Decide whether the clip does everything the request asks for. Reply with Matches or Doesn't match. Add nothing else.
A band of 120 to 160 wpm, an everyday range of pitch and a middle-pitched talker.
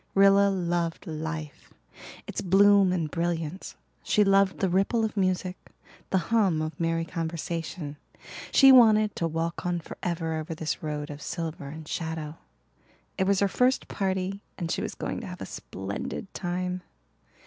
Matches